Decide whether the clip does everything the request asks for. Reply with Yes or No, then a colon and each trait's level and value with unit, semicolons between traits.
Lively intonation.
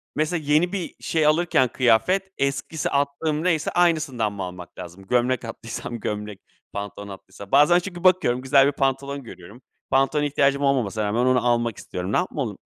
Yes: wide, 5.8 semitones